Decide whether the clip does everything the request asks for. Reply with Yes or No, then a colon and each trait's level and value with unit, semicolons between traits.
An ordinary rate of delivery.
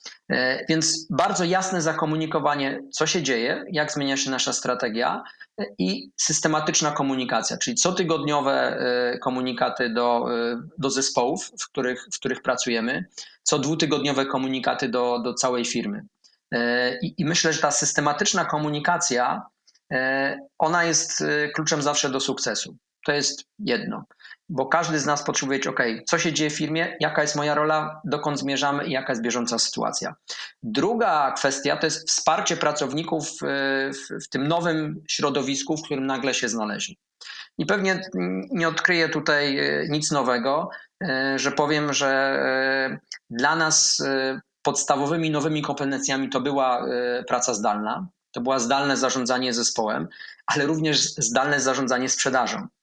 Yes: average, 130 wpm